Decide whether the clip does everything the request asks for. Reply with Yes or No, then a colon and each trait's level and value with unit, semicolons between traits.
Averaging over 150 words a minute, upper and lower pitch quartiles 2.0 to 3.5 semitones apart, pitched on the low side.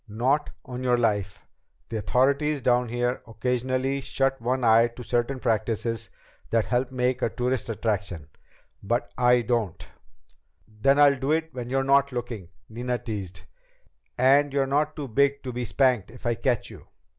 Yes: average, 160 wpm; average, 2.8 semitones; low, 125 Hz